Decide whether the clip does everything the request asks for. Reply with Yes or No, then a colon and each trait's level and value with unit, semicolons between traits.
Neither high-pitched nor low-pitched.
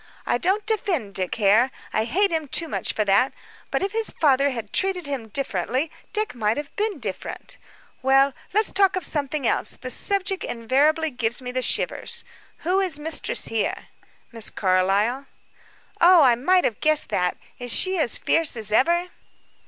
No: very high, 280 Hz